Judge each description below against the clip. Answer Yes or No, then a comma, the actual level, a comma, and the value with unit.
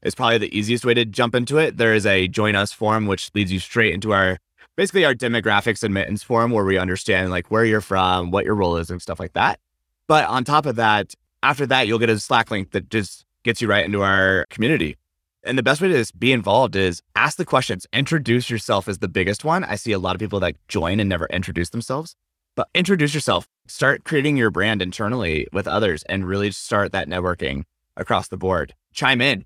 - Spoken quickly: Yes, fast, 225 wpm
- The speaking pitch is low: Yes, low, 105 Hz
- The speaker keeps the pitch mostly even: No, average, 4.0 semitones